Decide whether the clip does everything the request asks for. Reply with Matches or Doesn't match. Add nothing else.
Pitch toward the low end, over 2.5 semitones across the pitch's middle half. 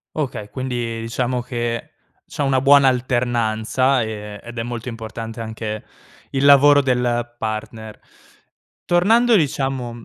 Matches